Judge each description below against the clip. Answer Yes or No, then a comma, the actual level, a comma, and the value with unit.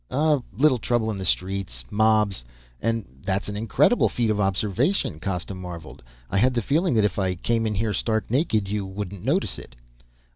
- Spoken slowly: No, average, 185 wpm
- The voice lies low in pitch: Yes, low, 105 Hz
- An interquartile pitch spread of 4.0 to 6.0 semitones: No, average, 3.5 semitones